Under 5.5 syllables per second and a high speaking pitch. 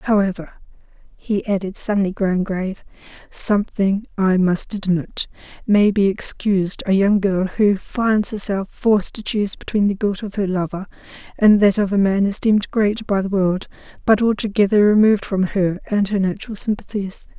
Yes: 5.1 syllables/s; high, 200 Hz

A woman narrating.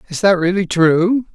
No: male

